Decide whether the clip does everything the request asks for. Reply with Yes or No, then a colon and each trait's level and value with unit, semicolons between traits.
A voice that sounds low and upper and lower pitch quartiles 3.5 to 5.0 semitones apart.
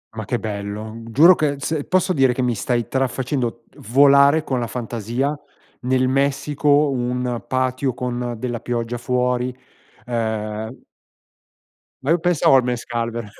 No: low, 125 Hz; average, 2.7 semitones